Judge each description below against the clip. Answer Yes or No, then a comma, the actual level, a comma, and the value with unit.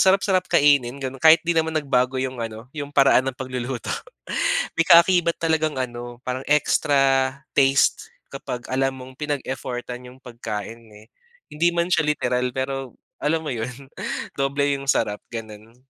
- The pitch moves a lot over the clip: No, average, 3.0 semitones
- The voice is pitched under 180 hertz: Yes, low, 135 Hz